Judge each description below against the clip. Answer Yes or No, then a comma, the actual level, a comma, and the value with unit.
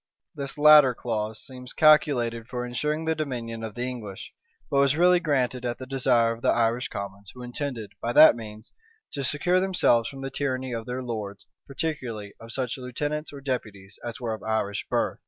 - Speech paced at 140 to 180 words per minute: No, average, 190 wpm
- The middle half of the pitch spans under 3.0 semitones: No, average, 3.6 semitones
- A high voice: No, low, 125 Hz